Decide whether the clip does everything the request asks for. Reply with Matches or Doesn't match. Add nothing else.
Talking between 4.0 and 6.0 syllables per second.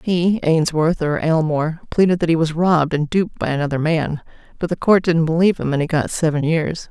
Matches